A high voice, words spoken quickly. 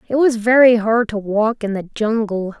Yes: high, 225 Hz; fast, 210 wpm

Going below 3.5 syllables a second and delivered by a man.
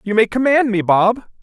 No: 4.9 syllables/s; male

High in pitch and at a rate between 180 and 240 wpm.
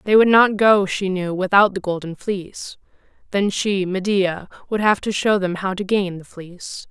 Yes: high, 195 Hz; average, 200 wpm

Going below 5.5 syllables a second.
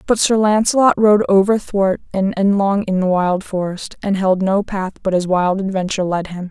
Yes: 5.0 syllables/s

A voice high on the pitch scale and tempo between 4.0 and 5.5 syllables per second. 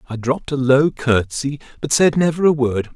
No: low, 135 Hz; 5.1 syllables/s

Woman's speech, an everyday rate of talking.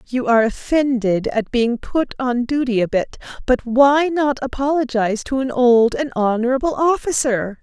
Yes: female; average, 155 wpm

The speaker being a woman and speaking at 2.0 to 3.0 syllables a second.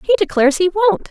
No: female; 6.1 syllables/s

